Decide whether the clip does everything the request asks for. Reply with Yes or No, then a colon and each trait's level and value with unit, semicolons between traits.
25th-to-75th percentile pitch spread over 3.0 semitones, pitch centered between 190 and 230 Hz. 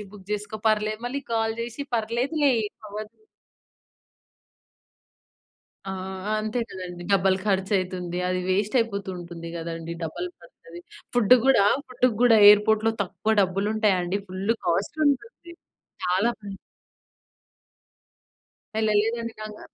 Yes: average, 3.4 semitones; high, 210 Hz